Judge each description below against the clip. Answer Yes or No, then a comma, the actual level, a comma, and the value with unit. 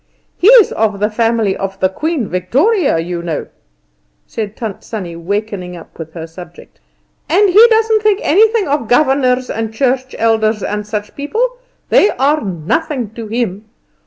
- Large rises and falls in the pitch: Yes, wide, 7.5 semitones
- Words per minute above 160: No, average, 155 wpm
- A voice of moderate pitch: No, high, 225 Hz